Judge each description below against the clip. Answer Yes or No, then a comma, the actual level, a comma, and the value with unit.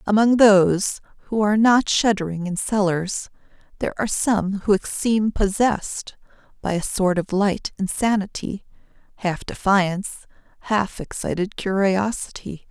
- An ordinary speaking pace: No, slow, 120 wpm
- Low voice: No, high, 200 Hz